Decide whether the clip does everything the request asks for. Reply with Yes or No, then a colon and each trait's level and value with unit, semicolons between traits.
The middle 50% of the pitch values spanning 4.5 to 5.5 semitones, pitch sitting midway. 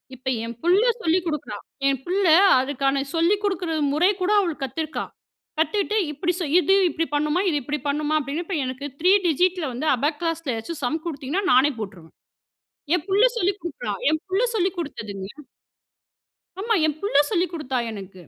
No: average, 4.8 semitones; very high, 315 Hz